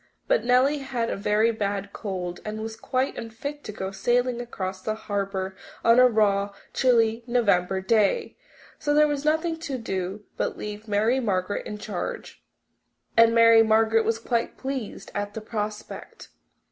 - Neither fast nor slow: Yes, average, 160 wpm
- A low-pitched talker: No, high, 220 Hz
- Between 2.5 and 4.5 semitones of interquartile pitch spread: Yes, average, 3.4 semitones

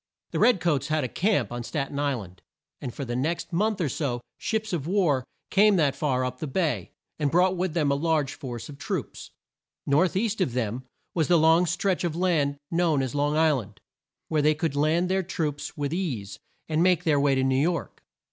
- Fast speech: Yes, fast, 215 wpm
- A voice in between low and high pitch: Yes, medium, 155 Hz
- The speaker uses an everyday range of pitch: Yes, average, 4.3 semitones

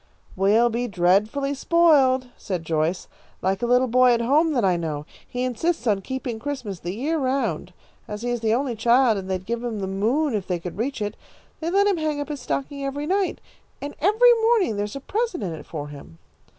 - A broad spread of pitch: Yes, wide, 6.4 semitones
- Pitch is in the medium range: No, high, 245 Hz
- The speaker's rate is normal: No, fast, 215 wpm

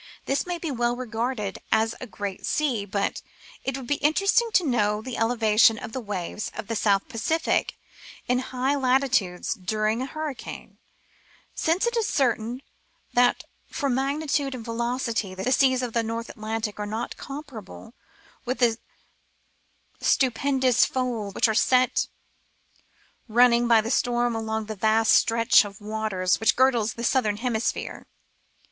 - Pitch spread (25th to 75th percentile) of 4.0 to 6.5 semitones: No, average, 3.1 semitones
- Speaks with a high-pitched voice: Yes, high, 235 Hz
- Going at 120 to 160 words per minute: Yes, average, 150 wpm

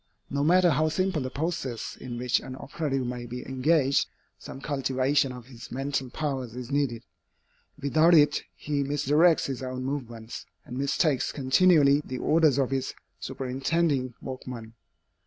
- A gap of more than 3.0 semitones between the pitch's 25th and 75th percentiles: No, average, 2.7 semitones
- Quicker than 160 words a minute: No, average, 145 wpm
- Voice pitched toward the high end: No, low, 135 Hz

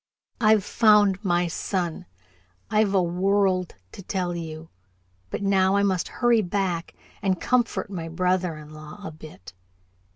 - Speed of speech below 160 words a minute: Yes, average, 140 wpm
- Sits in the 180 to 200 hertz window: Yes, medium, 185 Hz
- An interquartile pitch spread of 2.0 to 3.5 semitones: Yes, average, 2.9 semitones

